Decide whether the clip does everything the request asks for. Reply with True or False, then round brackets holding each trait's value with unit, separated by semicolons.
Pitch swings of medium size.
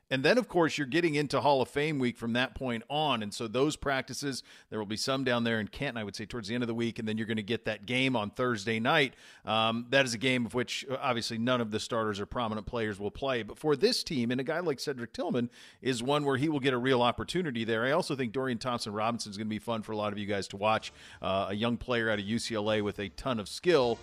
True (3.4 semitones)